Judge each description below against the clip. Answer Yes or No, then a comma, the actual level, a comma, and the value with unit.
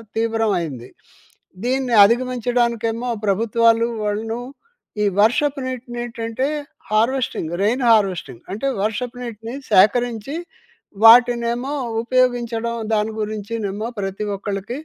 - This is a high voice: Yes, high, 230 Hz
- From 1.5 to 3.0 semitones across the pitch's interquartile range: Yes, narrow, 2.6 semitones